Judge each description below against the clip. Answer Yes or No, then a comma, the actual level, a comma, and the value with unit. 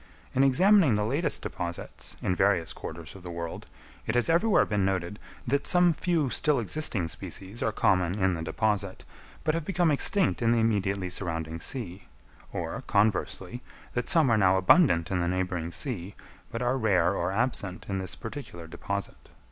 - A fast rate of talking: No, average, 170 wpm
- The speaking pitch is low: Yes, low, 100 Hz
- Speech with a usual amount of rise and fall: No, wide, 6.4 semitones